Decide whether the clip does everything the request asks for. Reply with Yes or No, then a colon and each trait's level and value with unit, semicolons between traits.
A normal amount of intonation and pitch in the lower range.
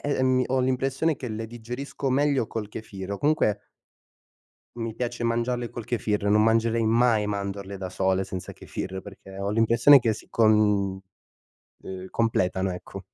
Yes: average, 3.6 semitones; low, 110 Hz